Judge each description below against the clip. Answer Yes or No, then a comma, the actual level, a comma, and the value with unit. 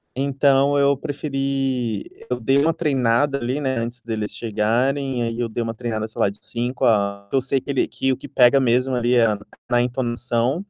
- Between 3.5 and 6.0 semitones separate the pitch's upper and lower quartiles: No, average, 2.8 semitones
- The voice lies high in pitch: No, low, 125 Hz